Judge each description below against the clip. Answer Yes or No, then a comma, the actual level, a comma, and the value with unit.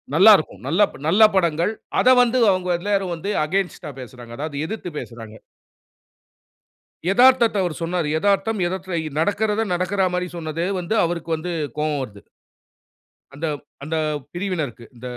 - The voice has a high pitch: No, medium, 175 Hz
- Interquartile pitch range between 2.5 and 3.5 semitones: No, average, 4.5 semitones